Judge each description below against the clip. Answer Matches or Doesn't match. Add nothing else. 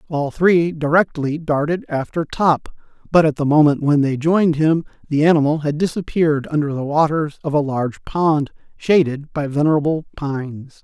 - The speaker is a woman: Doesn't match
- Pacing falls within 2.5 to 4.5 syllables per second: Doesn't match